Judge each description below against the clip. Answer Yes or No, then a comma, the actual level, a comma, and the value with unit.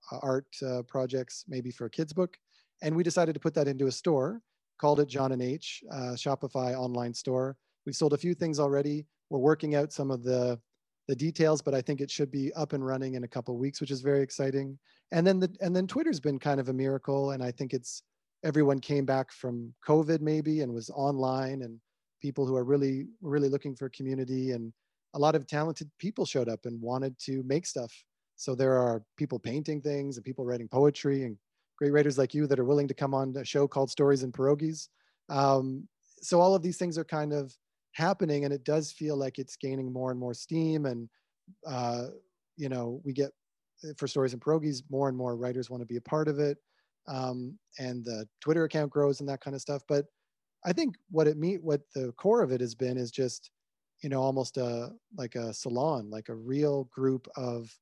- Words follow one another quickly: Yes, fast, 220 wpm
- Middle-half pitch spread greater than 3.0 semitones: No, narrow, 2.6 semitones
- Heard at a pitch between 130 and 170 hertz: Yes, medium, 140 Hz